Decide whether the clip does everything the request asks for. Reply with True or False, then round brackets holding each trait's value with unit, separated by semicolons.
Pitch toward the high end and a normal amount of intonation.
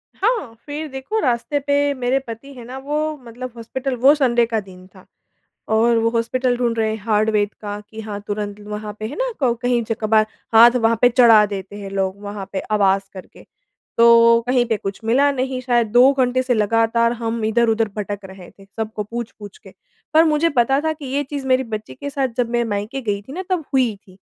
True (230 Hz; 3.7 semitones)